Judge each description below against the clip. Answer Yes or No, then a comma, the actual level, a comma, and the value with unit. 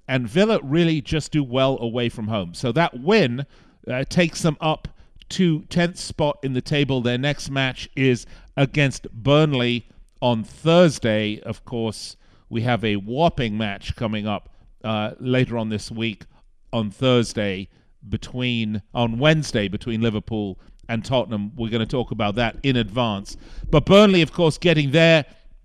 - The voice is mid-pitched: No, low, 120 Hz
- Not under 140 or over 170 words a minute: Yes, average, 155 wpm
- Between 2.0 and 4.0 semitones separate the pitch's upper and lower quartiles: No, average, 5.1 semitones